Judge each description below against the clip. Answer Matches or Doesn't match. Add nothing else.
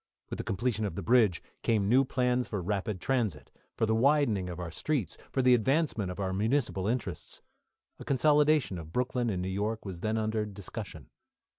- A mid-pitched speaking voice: Doesn't match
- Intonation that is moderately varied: Matches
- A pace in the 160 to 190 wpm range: Matches